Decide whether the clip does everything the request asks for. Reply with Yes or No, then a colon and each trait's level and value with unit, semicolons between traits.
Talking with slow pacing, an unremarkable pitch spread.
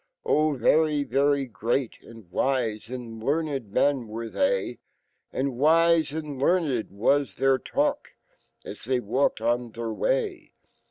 Yes: slow, 130 wpm; average, 4.6 semitones